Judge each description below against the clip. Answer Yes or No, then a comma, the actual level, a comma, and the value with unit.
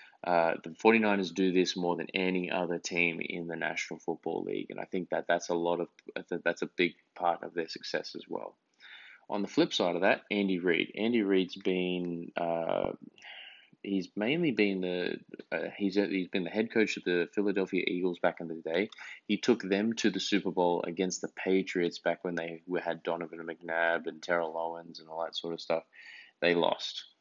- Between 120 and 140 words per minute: No, fast, 205 wpm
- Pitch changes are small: Yes, narrow, 2.3 semitones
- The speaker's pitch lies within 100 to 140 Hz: No, very low, 90 Hz